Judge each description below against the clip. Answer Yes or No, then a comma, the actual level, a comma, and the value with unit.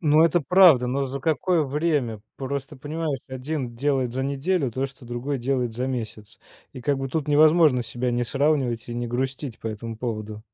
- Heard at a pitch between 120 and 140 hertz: Yes, low, 135 Hz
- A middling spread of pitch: Yes, average, 3.4 semitones